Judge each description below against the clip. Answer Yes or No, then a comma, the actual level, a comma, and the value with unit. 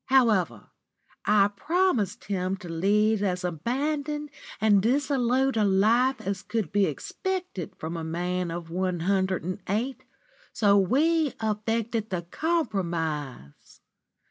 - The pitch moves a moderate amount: No, wide, 5.7 semitones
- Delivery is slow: Yes, slow, 120 wpm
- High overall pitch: Yes, high, 205 Hz